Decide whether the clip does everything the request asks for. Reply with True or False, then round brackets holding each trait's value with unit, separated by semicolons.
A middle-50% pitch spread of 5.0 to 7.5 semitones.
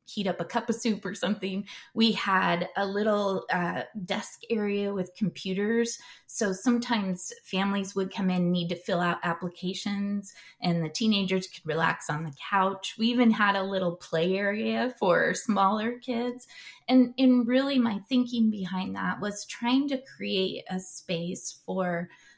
False (3.7 semitones)